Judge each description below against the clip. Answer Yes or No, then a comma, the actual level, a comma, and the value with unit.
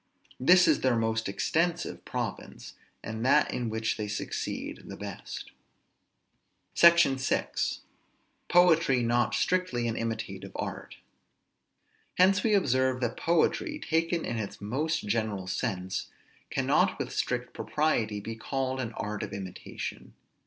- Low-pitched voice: Yes, low, 125 Hz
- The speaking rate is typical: No, slow, 130 wpm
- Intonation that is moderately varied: No, wide, 6.8 semitones